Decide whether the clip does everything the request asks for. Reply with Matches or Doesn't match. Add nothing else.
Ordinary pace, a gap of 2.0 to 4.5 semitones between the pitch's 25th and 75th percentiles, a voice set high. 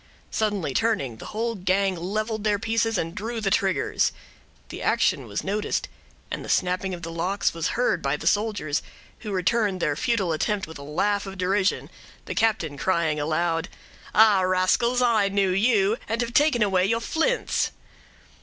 Matches